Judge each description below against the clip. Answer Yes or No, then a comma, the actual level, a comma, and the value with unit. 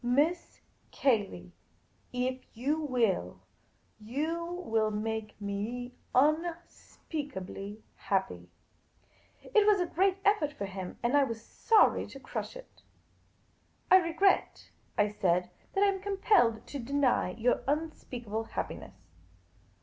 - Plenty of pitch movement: Yes, wide, 7.8 semitones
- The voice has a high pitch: Yes, very high, 250 Hz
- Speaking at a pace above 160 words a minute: No, slow, 135 wpm